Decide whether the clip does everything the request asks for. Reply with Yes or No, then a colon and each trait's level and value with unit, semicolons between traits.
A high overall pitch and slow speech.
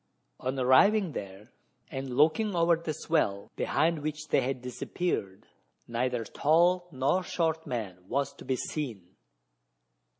No: medium, 140 Hz; slow, 130 wpm